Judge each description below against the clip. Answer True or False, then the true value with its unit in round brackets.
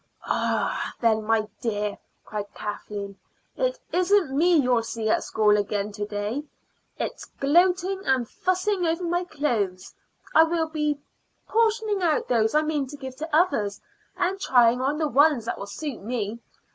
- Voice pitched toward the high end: True (275 Hz)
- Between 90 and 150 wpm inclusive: False (160 wpm)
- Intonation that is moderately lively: False (7.9 semitones)